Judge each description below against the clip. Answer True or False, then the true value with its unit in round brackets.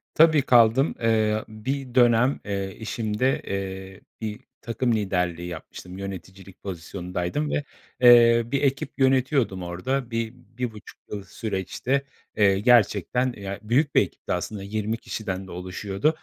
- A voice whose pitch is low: True (110 Hz)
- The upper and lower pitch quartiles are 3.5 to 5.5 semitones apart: True (4.4 semitones)